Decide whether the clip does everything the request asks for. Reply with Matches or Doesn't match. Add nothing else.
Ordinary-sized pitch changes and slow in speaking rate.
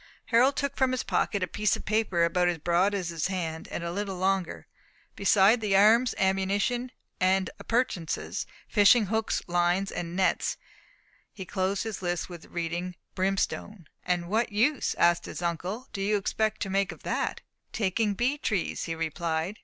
Doesn't match